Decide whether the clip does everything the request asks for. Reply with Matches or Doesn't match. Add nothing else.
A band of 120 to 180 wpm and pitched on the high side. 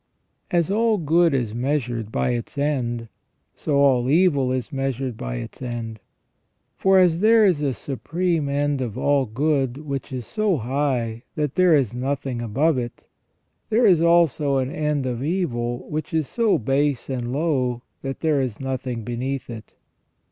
Doesn't match